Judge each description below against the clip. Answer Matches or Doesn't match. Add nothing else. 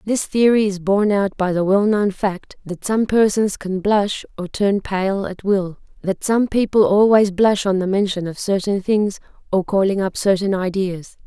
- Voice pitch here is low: Doesn't match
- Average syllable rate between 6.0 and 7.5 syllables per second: Doesn't match